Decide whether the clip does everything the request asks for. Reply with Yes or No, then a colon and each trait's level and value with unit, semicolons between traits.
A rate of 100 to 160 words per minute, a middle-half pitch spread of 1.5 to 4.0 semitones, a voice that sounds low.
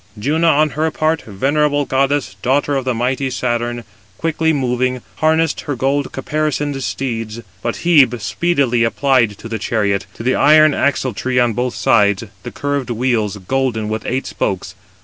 Yes: average, 150 wpm; average, 3.6 semitones; low, 130 Hz